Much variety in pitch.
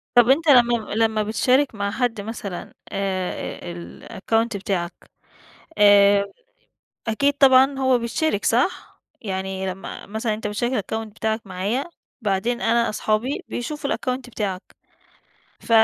No: average, 3.6 semitones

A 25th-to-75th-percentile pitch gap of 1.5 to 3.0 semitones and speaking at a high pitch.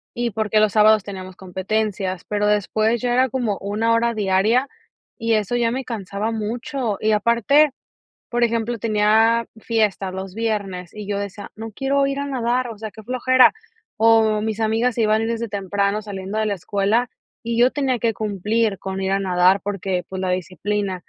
Yes: average, 2.7 semitones; high, 215 Hz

